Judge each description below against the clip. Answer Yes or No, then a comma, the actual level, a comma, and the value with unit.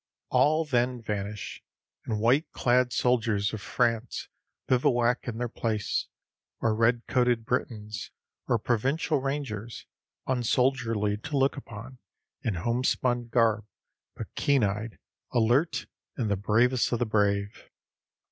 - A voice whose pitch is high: No, low, 120 Hz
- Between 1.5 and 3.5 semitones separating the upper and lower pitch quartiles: Yes, average, 2.9 semitones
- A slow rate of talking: Yes, slow, 125 wpm